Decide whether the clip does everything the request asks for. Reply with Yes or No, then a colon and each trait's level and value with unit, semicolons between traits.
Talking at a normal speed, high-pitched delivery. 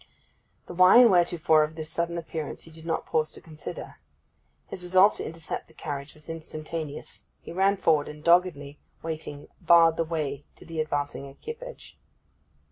No: average, 165 wpm; medium, 160 Hz